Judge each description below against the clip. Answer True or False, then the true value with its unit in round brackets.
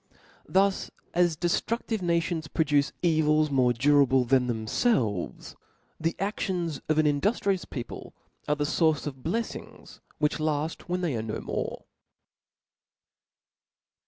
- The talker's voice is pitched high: False (155 Hz)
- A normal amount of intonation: True (4.1 semitones)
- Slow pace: True (125 wpm)